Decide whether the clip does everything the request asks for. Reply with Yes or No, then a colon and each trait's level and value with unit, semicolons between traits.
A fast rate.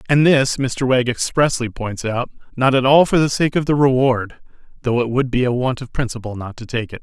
Yes: fast, 230 wpm